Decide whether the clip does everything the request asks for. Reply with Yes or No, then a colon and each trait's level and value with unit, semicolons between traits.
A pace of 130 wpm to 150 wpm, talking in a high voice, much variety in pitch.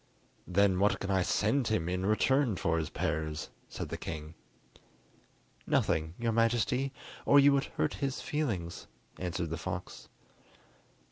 No: average, 140 wpm; very low, 95 Hz; wide, 6.3 semitones